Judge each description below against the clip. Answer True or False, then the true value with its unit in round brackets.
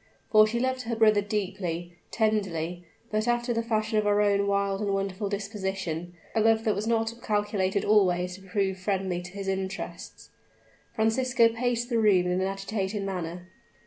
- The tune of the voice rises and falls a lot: False (2.6 semitones)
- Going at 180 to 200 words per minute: False (170 wpm)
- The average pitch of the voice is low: False (200 Hz)